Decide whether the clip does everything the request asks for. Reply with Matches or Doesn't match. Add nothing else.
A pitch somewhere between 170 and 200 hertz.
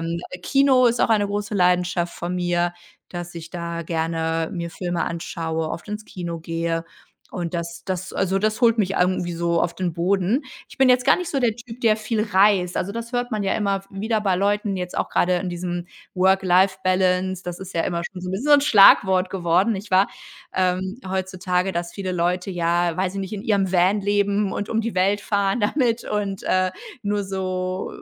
Matches